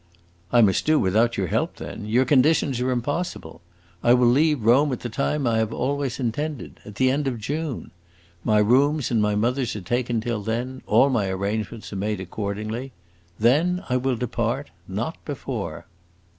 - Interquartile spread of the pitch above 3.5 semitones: Yes, average, 4.0 semitones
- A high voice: No, low, 120 Hz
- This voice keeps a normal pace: Yes, average, 175 wpm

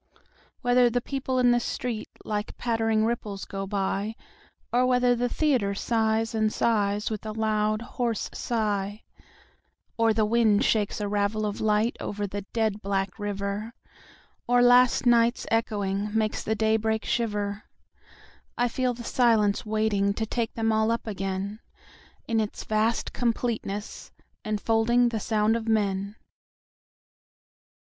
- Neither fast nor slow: No, slow, 115 wpm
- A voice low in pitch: No, high, 220 Hz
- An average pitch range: No, narrow, 2.1 semitones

